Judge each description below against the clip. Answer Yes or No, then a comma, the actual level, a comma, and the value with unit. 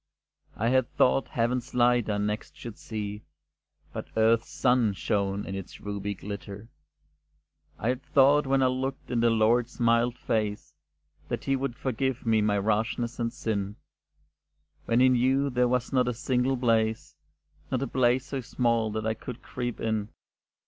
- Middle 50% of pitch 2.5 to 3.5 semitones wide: Yes, average, 2.8 semitones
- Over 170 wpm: No, average, 160 wpm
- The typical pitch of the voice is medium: No, low, 115 Hz